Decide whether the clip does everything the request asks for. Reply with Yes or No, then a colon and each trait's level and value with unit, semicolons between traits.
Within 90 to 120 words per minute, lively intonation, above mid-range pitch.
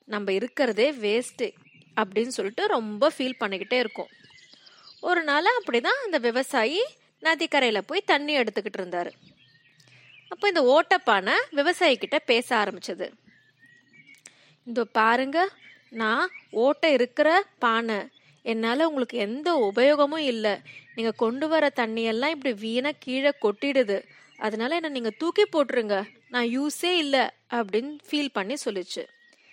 Yes: average, 115 wpm; wide, 5.9 semitones; very high, 260 Hz